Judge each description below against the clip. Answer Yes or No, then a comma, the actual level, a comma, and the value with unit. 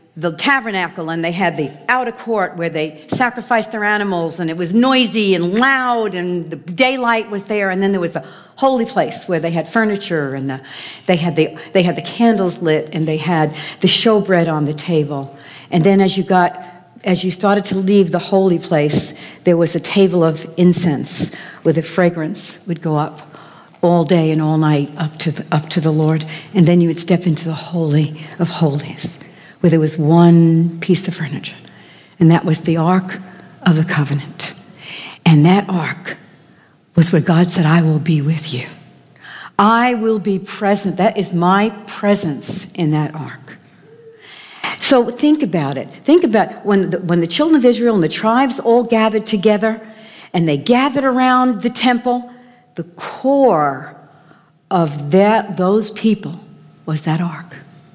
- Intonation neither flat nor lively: Yes, average, 4.4 semitones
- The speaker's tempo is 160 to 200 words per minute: Yes, average, 180 wpm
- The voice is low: No, medium, 175 Hz